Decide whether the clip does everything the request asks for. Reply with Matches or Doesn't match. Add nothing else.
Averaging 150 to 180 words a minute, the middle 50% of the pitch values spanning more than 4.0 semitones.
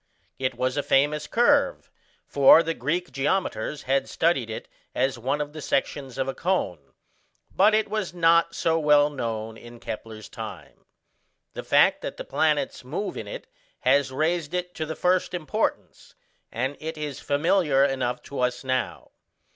Matches